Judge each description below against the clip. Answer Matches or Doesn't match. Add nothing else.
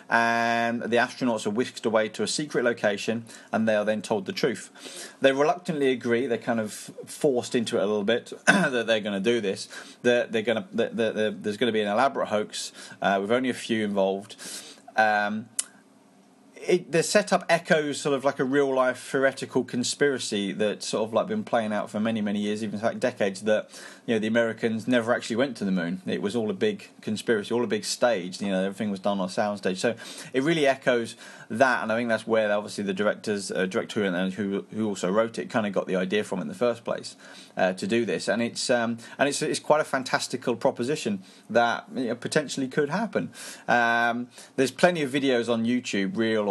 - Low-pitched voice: Matches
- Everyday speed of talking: Doesn't match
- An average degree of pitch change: Matches